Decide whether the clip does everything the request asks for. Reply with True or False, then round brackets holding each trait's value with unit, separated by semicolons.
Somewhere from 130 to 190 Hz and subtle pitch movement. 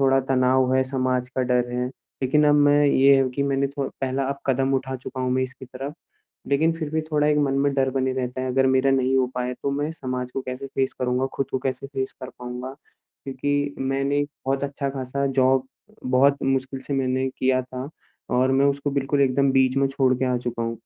True (135 Hz; 1.3 semitones)